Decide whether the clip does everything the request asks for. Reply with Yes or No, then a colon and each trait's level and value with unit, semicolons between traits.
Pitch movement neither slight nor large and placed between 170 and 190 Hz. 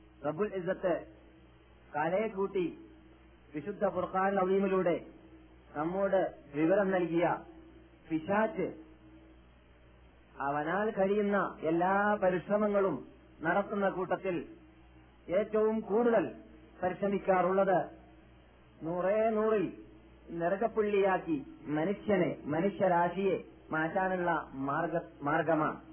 Yes: average, 4.8 semitones; medium, 185 Hz